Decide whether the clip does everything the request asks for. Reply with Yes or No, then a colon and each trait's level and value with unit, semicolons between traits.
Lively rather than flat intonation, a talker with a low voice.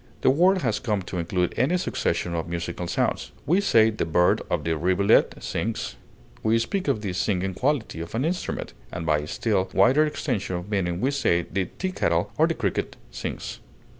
Yes: wide, 6.9 semitones; low, 100 Hz